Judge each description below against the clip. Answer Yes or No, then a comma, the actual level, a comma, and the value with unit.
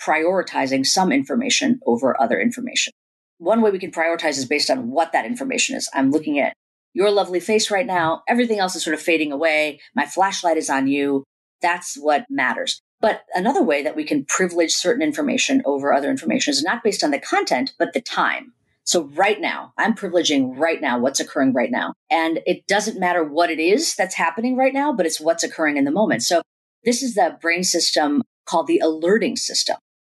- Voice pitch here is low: No, medium, 185 Hz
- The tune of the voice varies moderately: No, wide, 7.8 semitones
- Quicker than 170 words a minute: Yes, average, 200 wpm